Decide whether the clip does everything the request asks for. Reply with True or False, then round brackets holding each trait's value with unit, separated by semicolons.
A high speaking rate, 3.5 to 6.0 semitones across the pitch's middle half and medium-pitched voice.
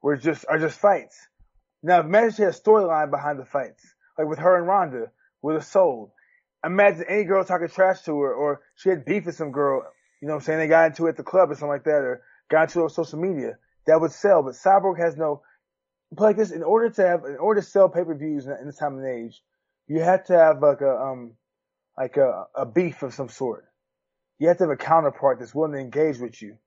True (245 wpm; 4.2 semitones; 160 Hz)